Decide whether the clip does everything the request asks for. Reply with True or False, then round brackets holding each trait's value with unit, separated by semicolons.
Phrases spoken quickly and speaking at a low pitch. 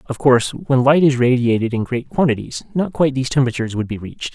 True (220 wpm; 130 Hz)